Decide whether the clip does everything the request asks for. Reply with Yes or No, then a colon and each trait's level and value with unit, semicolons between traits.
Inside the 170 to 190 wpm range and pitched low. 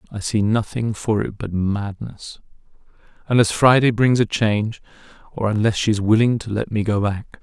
Yes: average, 180 wpm; low, 110 Hz